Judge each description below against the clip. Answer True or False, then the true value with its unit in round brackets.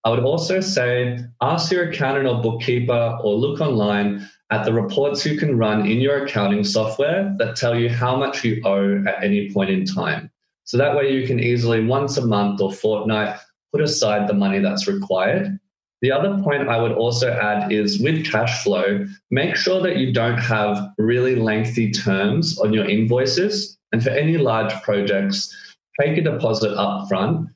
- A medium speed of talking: True (185 wpm)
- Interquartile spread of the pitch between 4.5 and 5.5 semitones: True (5.1 semitones)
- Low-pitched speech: True (120 Hz)